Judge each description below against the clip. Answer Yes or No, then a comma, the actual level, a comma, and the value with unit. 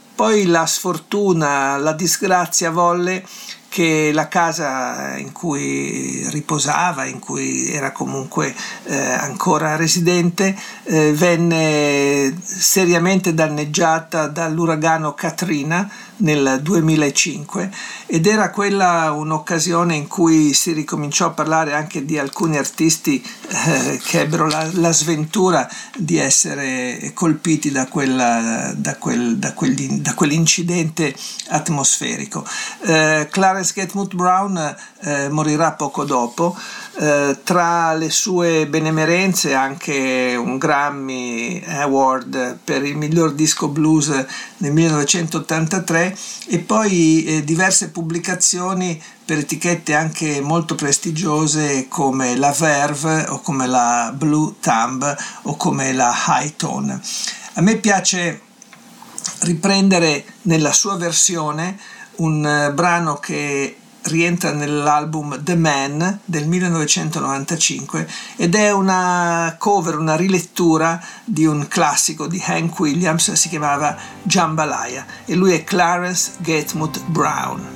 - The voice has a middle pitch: Yes, medium, 165 Hz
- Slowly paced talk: Yes, slow, 110 wpm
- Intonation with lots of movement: No, average, 3.2 semitones